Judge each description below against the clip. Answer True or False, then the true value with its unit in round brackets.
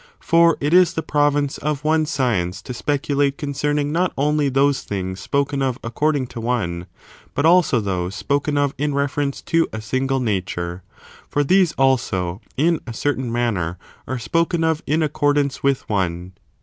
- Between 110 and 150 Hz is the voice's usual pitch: True (140 Hz)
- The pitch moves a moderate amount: True (4.5 semitones)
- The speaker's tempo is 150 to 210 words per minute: True (160 wpm)